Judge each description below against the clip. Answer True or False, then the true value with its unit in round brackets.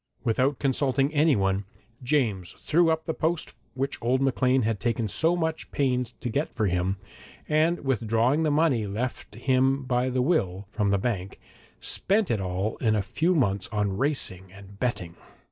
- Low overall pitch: True (125 Hz)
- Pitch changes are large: True (6.0 semitones)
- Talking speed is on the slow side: False (165 wpm)